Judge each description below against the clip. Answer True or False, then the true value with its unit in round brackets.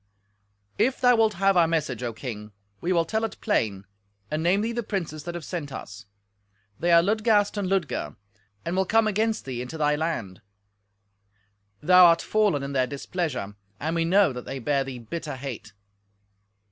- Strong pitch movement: True (6.5 semitones)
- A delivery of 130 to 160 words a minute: False (180 wpm)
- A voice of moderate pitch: True (165 Hz)